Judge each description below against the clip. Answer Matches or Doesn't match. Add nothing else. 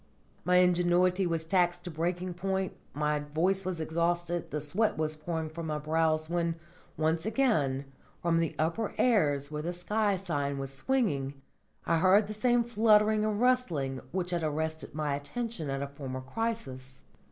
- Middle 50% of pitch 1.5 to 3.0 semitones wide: Doesn't match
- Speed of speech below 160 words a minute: Doesn't match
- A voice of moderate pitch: Matches